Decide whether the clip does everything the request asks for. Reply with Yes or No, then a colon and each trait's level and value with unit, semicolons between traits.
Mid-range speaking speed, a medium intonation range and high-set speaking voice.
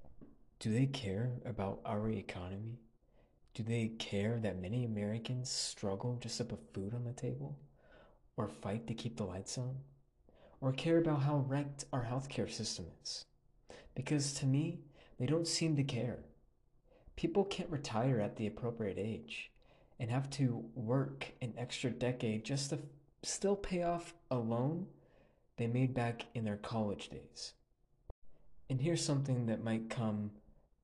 No: average, 150 wpm; average, 3.9 semitones; low, 120 Hz